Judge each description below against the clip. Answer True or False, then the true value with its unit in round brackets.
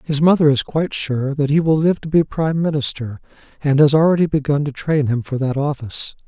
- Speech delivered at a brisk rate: True (220 wpm)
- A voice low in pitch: False (145 Hz)